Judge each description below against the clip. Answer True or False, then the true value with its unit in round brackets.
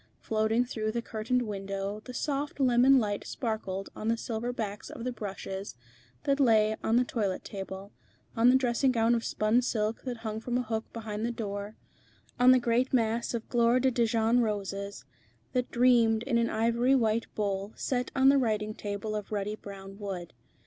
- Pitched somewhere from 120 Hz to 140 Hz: False (225 Hz)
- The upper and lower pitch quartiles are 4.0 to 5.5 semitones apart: False (2.7 semitones)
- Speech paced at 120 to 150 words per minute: False (185 wpm)